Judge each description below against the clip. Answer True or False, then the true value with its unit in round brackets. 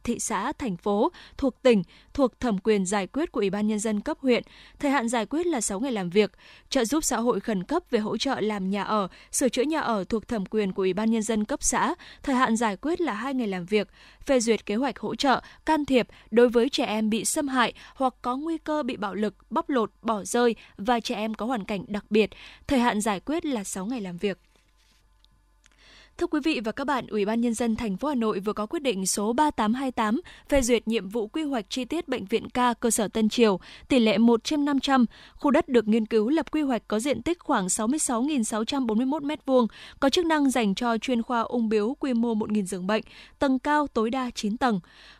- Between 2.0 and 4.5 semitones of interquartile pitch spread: True (4.2 semitones)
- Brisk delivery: False (240 wpm)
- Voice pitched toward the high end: True (235 Hz)